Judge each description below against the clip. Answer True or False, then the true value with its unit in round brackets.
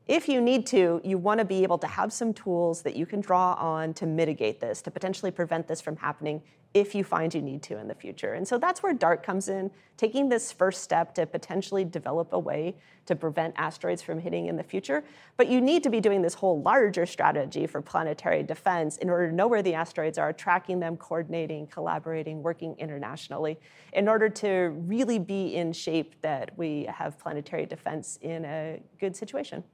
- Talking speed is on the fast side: True (210 wpm)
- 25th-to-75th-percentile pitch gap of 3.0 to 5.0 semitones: True (3.5 semitones)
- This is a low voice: False (175 Hz)